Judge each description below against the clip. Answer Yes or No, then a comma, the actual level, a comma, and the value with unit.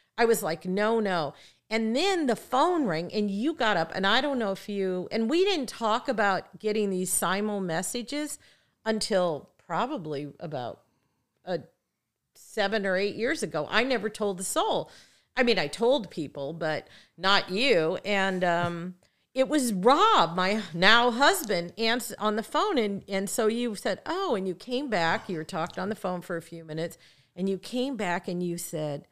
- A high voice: Yes, high, 200 Hz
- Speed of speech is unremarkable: Yes, average, 185 wpm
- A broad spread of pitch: No, average, 4.8 semitones